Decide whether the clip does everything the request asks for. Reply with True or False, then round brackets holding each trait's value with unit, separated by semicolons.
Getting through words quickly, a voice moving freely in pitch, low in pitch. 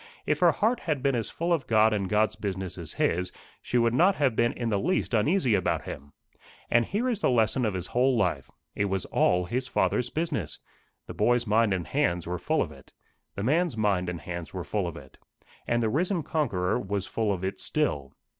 True (220 wpm; 5.9 semitones; 110 Hz)